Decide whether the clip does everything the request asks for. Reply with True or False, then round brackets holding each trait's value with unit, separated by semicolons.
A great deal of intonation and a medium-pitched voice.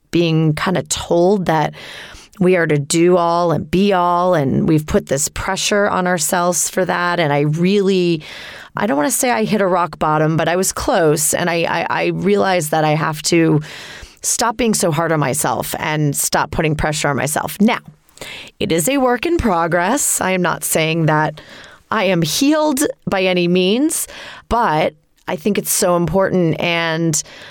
False (3.3 semitones; 175 Hz)